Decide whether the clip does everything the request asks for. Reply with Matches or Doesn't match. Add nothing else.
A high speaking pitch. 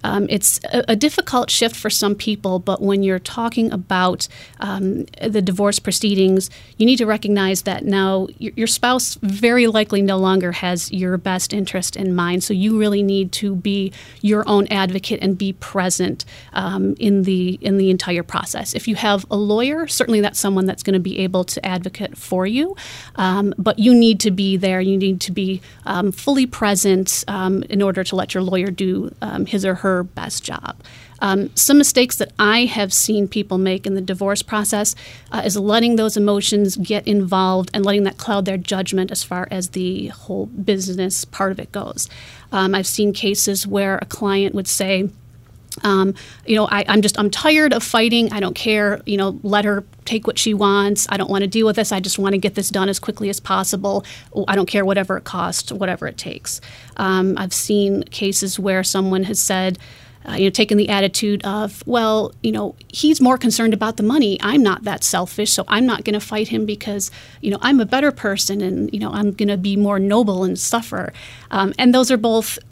Matches